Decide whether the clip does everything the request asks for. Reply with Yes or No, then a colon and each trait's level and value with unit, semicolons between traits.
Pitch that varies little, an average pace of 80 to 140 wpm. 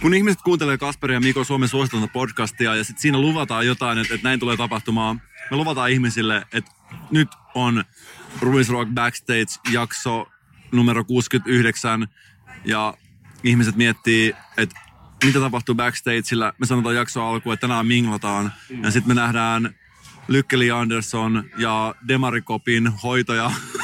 Yes: narrow, 2.2 semitones; average, 135 wpm